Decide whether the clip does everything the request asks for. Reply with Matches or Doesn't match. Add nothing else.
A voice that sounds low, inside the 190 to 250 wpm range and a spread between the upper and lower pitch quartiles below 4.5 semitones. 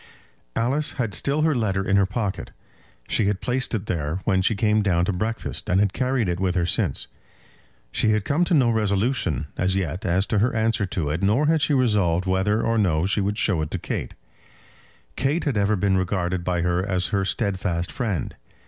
Matches